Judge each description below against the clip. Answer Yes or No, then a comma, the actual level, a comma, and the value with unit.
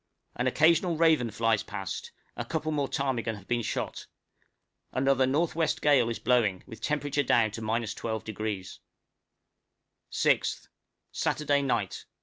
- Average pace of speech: No, slow, 125 wpm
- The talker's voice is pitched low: Yes, low, 125 Hz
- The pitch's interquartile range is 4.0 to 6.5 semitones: Yes, average, 4.7 semitones